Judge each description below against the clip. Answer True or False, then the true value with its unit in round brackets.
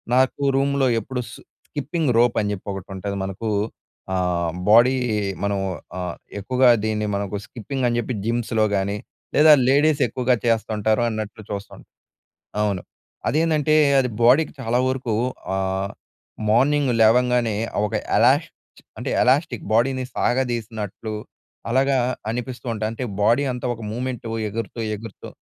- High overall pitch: False (120 Hz)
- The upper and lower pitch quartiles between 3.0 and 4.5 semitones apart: True (3.6 semitones)